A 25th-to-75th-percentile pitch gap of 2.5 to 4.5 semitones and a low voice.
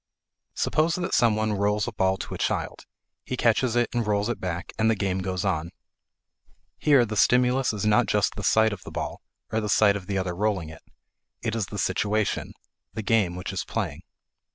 Yes: average, 3.0 semitones; low, 105 Hz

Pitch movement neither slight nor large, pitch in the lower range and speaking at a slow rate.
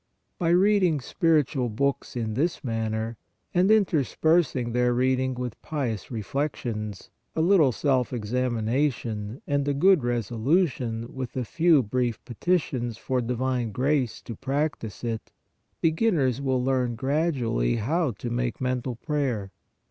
Yes: average, 4.2 semitones; low, 130 Hz; slow, 130 wpm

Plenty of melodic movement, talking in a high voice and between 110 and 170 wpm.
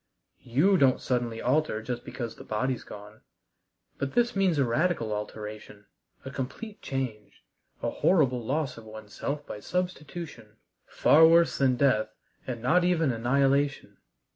No: wide, 5.7 semitones; low, 130 Hz; average, 140 wpm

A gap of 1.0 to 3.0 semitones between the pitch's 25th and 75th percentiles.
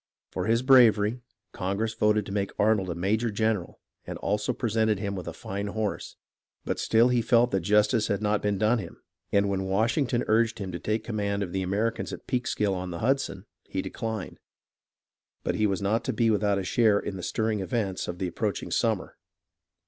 Yes: narrow, 2.4 semitones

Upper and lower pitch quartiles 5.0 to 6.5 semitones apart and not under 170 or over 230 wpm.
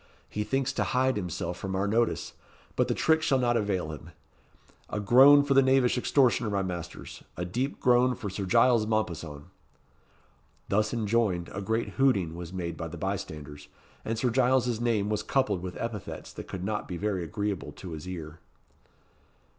Yes: average, 5.3 semitones; average, 175 wpm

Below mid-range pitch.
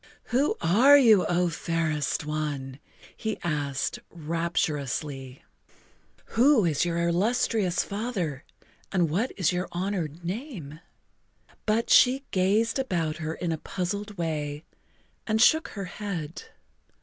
No: medium, 175 Hz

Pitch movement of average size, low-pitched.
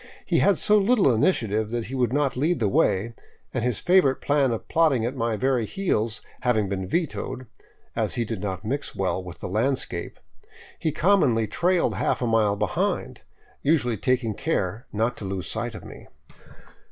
Yes: average, 4.7 semitones; low, 120 Hz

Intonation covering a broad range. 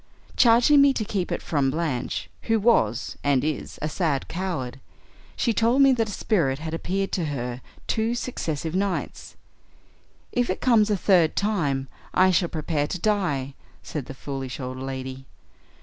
Yes: wide, 7.7 semitones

